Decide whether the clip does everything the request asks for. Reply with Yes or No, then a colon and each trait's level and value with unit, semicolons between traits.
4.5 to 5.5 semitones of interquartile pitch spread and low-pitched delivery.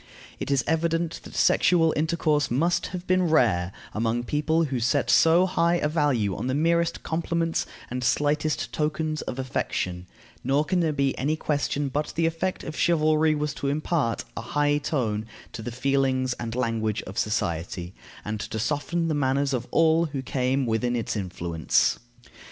No: average, 4.9 semitones; medium, 145 Hz